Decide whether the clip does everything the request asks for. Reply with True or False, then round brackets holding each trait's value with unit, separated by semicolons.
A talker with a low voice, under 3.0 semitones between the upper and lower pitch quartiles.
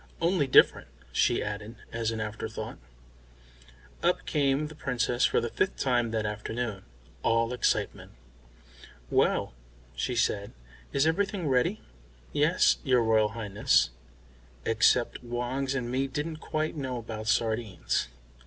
False (120 Hz; 3.8 semitones)